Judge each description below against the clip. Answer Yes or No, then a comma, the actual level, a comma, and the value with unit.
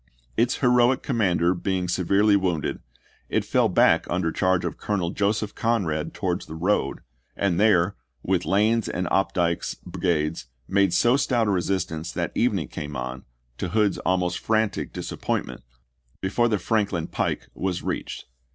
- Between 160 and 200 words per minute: No, average, 150 wpm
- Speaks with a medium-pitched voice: No, very low, 95 Hz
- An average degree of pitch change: Yes, average, 3.4 semitones